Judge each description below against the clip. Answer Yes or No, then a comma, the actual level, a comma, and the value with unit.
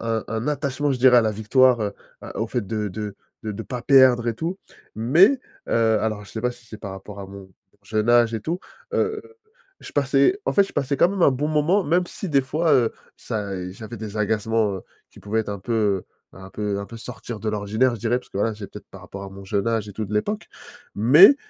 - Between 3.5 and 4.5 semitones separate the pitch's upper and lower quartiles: Yes, average, 3.9 semitones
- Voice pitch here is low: Yes, low, 115 Hz